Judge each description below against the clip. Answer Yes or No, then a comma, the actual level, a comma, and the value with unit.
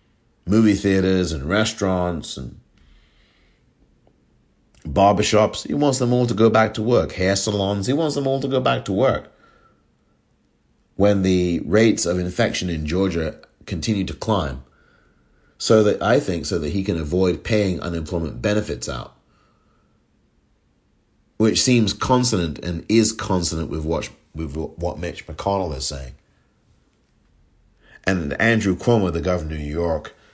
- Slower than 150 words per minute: Yes, average, 140 wpm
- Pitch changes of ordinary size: Yes, average, 4.6 semitones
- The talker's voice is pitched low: Yes, very low, 95 Hz